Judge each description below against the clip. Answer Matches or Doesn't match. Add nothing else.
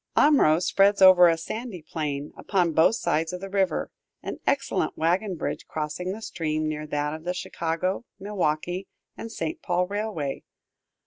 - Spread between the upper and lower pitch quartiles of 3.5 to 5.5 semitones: Matches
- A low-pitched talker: Doesn't match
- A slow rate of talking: Doesn't match